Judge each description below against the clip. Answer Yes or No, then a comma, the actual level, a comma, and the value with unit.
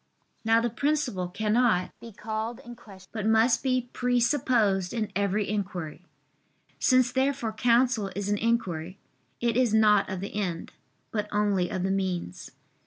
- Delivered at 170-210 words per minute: No, average, 150 wpm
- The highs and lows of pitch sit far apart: No, average, 3.6 semitones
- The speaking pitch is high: Yes, high, 215 Hz